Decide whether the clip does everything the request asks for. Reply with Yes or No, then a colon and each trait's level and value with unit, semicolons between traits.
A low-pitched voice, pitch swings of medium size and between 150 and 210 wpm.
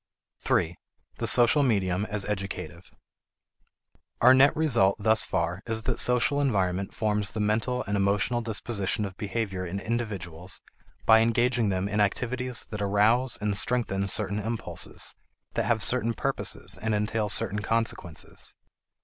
No: low, 105 Hz; average, 3.1 semitones; average, 140 wpm